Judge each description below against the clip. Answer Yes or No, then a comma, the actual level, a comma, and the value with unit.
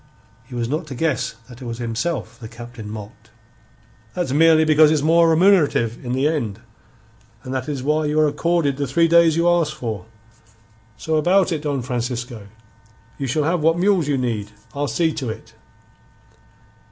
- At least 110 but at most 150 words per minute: No, average, 175 wpm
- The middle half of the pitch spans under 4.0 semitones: No, average, 5.1 semitones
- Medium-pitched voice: Yes, medium, 145 Hz